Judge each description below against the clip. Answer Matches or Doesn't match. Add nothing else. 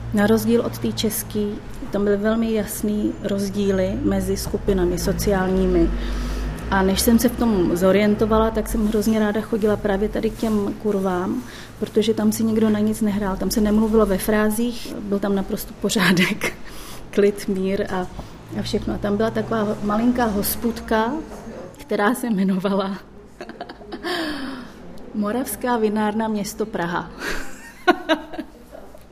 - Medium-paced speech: Matches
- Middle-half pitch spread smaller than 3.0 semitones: Matches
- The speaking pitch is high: Matches